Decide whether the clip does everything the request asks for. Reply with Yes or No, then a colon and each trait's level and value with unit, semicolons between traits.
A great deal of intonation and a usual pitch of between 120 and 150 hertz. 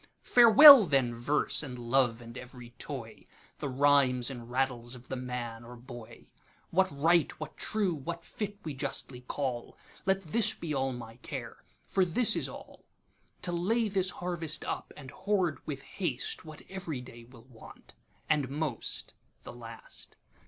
Yes: wide, 5.9 semitones; medium, 140 Hz